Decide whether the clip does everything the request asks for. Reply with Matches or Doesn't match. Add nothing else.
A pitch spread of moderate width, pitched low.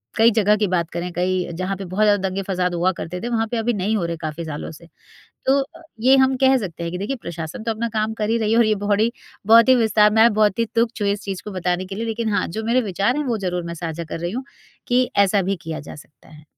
Doesn't match